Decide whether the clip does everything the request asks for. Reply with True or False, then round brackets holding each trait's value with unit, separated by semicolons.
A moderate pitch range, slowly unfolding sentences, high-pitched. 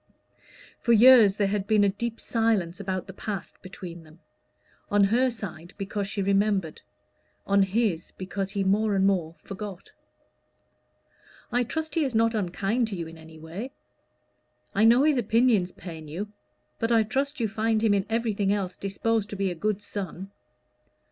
False (3.0 semitones; 170 wpm; 200 Hz)